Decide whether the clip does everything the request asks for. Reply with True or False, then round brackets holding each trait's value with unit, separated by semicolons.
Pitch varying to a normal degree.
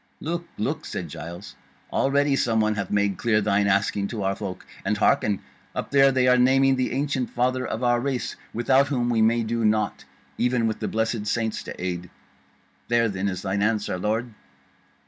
True (3.8 semitones)